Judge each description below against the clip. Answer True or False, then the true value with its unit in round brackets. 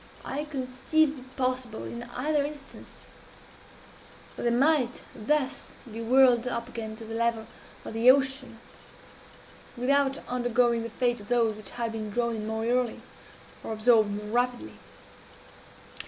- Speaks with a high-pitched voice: True (245 Hz)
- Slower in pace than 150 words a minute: True (140 wpm)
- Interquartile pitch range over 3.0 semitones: False (2.6 semitones)